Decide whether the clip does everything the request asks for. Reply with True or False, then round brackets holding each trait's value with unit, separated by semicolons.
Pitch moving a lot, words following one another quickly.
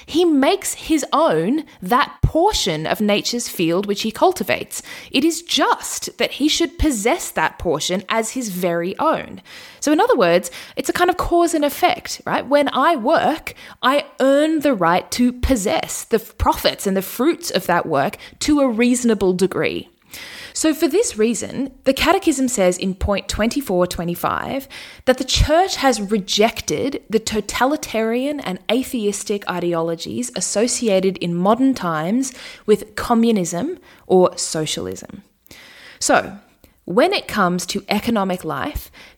False (7.3 semitones; 140 wpm)